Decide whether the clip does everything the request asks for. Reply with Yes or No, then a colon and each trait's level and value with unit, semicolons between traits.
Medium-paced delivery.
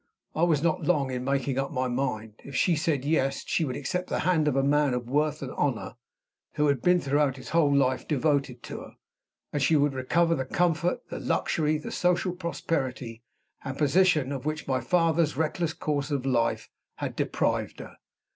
Yes: average, 195 wpm